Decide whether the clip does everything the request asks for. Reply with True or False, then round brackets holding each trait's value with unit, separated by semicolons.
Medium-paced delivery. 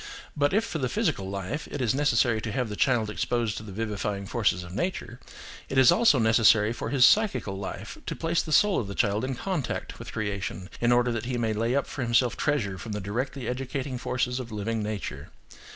False (215 wpm)